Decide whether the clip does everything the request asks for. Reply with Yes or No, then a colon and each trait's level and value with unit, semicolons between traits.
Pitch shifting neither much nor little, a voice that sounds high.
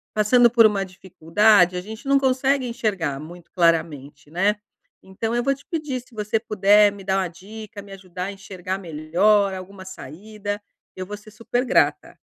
Yes: average, 3.3 semitones; high, 200 Hz